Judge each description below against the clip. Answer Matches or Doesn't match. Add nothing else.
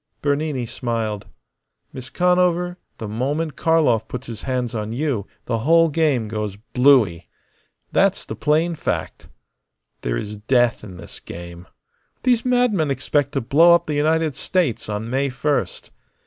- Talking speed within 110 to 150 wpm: Matches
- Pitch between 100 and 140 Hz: Matches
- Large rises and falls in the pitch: Matches